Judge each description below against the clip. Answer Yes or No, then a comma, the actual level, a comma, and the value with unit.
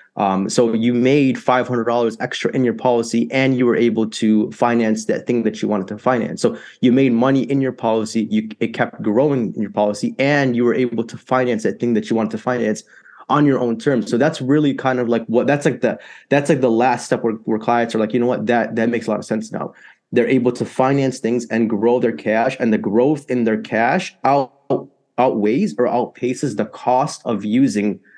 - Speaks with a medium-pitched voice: No, low, 120 Hz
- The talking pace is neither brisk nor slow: No, fast, 230 wpm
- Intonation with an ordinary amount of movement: No, narrow, 2.3 semitones